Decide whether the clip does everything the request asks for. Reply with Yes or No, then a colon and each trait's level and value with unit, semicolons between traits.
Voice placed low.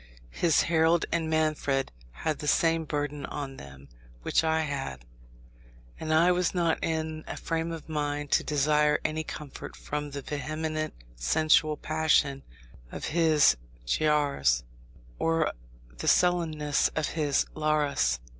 No: medium, 155 Hz